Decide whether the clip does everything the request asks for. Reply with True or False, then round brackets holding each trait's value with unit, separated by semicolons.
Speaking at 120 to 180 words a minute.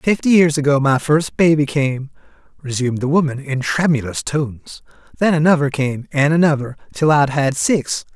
True (160 wpm)